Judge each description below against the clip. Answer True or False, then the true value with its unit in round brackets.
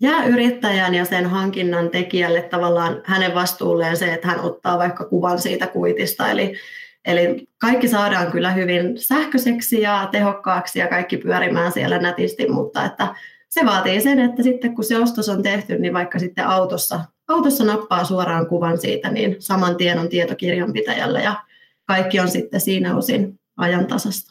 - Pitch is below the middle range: False (190 Hz)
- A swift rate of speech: True (160 wpm)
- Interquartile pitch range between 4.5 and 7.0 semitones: True (4.9 semitones)